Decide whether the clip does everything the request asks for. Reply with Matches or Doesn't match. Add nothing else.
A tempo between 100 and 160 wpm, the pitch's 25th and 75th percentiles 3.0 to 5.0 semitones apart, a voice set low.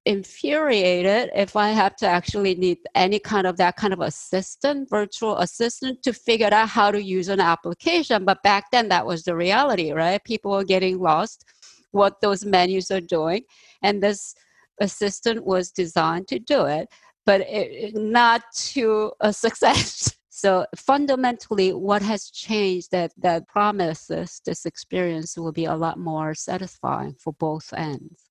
Doesn't match